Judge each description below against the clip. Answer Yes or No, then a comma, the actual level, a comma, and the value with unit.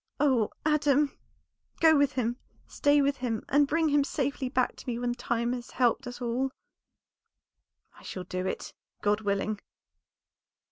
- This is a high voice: Yes, very high, 255 Hz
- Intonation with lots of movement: No, average, 3.4 semitones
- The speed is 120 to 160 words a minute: Yes, average, 150 wpm